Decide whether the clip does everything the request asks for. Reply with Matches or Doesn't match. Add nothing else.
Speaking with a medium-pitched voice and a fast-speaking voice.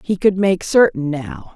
Doesn't match